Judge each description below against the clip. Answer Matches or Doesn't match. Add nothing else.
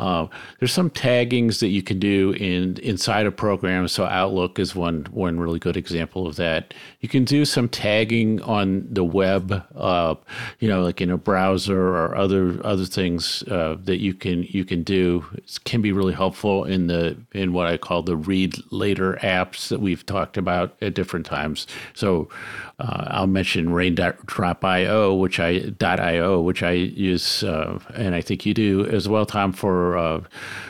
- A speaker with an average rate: Matches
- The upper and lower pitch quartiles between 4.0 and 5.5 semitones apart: Doesn't match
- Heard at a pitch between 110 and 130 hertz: Doesn't match